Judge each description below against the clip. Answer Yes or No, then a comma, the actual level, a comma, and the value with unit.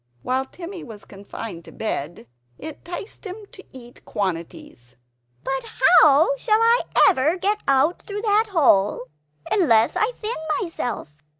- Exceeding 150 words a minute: No, slow, 135 wpm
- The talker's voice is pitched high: Yes, very high, 300 Hz